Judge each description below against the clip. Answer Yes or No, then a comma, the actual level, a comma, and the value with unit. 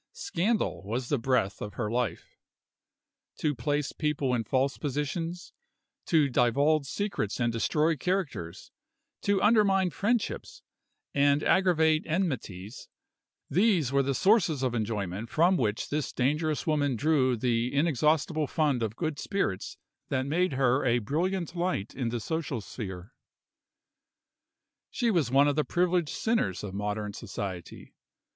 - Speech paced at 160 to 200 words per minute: No, slow, 135 wpm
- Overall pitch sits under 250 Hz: Yes, medium, 140 Hz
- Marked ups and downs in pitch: Yes, wide, 5.9 semitones